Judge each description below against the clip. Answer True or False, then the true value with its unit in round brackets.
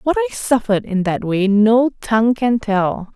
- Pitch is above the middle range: True (225 Hz)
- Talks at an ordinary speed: True (190 wpm)